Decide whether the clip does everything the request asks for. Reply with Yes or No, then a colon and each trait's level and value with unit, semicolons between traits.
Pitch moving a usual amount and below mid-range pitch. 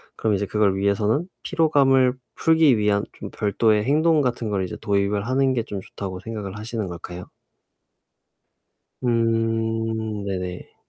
Yes: average, 3.6 semitones; low, 110 Hz